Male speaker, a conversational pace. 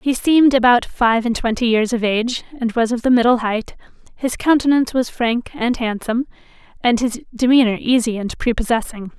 No: female; average, 175 wpm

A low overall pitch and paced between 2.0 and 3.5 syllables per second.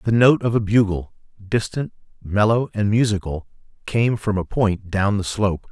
No: low, 105 Hz; 4.8 syllables/s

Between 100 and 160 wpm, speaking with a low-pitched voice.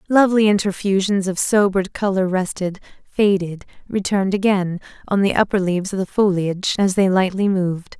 No: average, 150 wpm; high, 195 Hz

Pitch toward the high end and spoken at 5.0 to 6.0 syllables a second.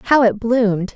Yes: high, 225 Hz; 5.3 syllables/s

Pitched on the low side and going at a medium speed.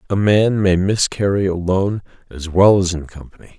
Yes: very low, 95 Hz; average, 165 wpm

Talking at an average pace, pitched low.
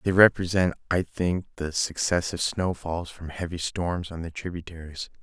Yes: average, 150 wpm; very low, 85 Hz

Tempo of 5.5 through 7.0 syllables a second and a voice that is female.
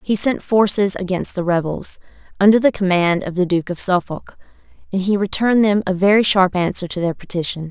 Yes: 5.6 syllables/s; female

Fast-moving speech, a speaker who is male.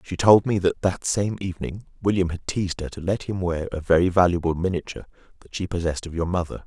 Yes: fast, 225 wpm; male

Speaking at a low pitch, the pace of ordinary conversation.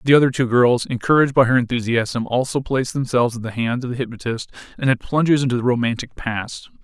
No: low, 125 Hz; fast, 210 wpm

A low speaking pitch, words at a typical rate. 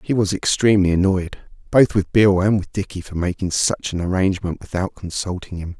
Yes: very low, 95 Hz; average, 185 wpm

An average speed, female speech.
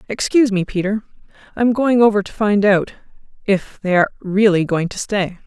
Yes: average, 175 wpm; female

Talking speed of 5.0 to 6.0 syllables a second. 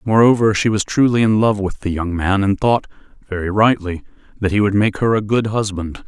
Yes: 5.3 syllables/s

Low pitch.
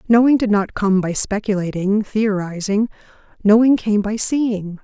No: high, 210 Hz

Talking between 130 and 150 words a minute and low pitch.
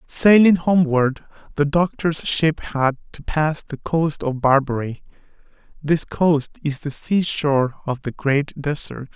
No: average, 140 wpm; medium, 150 Hz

